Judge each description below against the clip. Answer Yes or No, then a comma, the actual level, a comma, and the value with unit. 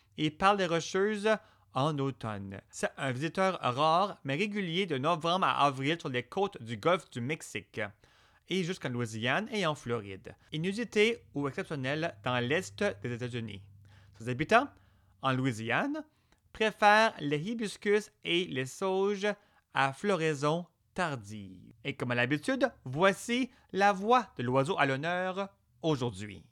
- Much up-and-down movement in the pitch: Yes, wide, 8.1 semitones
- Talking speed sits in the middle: No, slow, 140 wpm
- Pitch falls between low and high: Yes, medium, 155 Hz